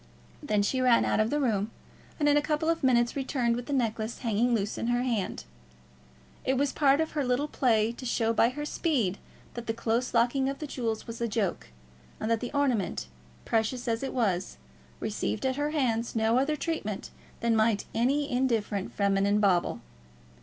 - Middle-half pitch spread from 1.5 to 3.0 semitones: No, average, 3.5 semitones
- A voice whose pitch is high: Yes, high, 235 Hz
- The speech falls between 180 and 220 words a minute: Yes, average, 190 wpm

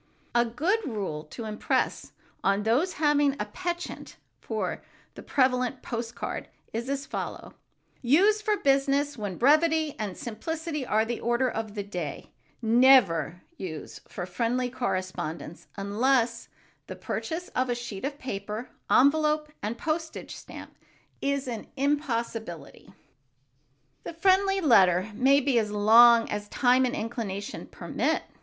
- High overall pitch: Yes, high, 245 Hz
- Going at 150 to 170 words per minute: No, slow, 135 wpm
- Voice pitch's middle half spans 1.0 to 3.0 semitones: No, average, 5.2 semitones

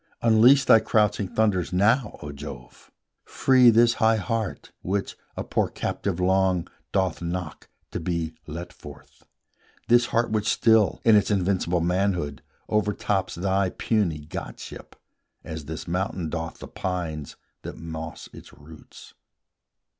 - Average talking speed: No, slow, 130 wpm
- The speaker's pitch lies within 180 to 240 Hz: No, very low, 95 Hz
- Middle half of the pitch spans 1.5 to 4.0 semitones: No, average, 4.6 semitones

